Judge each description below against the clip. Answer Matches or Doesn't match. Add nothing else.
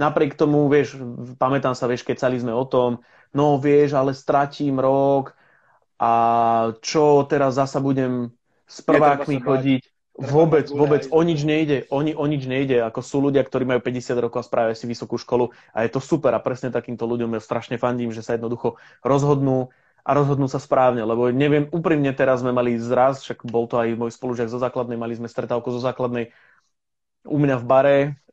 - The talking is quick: Matches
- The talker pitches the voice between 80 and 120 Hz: Doesn't match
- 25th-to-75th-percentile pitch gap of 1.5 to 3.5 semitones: Matches